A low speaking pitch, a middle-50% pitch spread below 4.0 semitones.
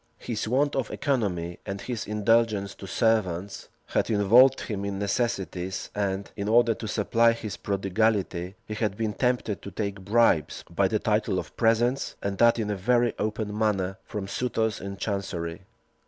Yes: low, 105 Hz; average, 2.8 semitones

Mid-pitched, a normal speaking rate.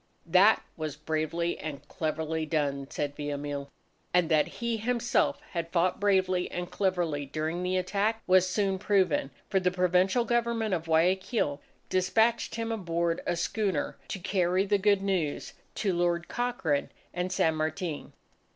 Yes: medium, 180 Hz; average, 145 wpm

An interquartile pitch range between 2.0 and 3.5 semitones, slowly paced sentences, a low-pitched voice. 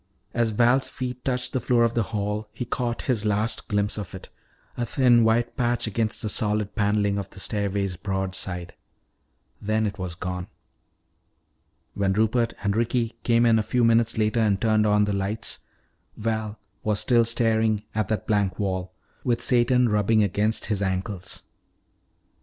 No: narrow, 2.6 semitones; average, 165 wpm; low, 110 Hz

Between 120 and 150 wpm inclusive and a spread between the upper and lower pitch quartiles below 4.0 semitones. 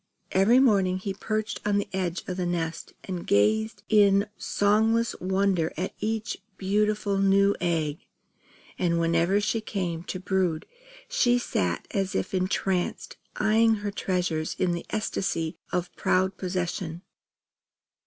Yes: slow, 135 wpm; average, 2.9 semitones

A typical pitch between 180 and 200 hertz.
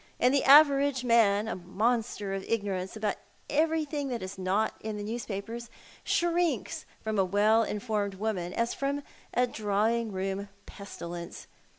No: high, 220 Hz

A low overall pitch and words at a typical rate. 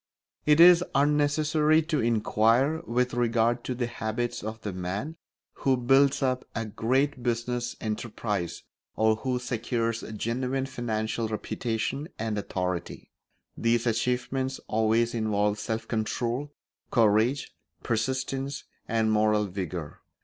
No: low, 120 Hz; slow, 115 wpm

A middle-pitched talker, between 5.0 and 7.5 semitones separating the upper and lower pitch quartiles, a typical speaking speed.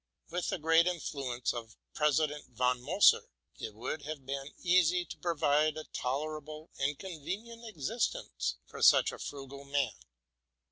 No: medium, 150 Hz; average, 3.7 semitones; average, 145 wpm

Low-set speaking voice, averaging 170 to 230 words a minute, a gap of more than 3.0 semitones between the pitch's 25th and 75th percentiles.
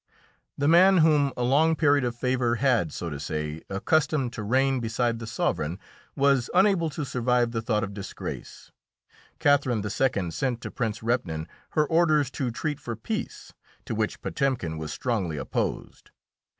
No: low, 125 Hz; average, 160 wpm; average, 5.0 semitones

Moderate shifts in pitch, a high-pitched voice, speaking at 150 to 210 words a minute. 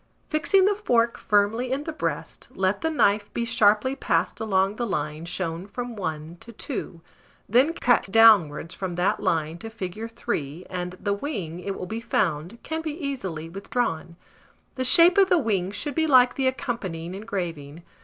No: wide, 6.1 semitones; high, 205 Hz; average, 175 wpm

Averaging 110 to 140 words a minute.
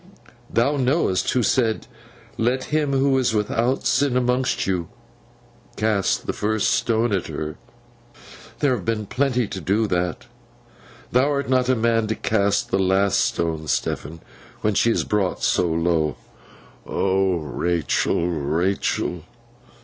Yes: slow, 135 wpm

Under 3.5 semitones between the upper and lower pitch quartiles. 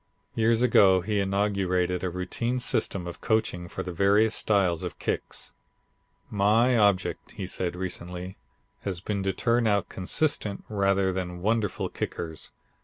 Yes: average, 2.9 semitones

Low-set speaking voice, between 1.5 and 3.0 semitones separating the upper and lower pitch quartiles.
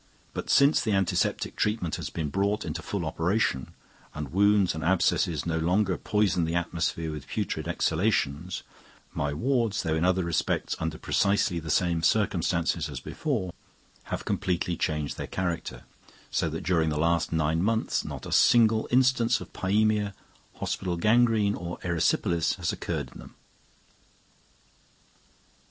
No: very low, 90 Hz; average, 4.3 semitones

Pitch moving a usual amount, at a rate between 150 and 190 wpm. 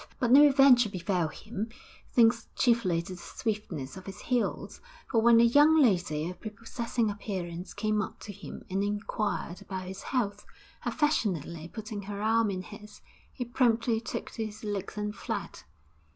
Yes: average, 3.6 semitones; average, 165 wpm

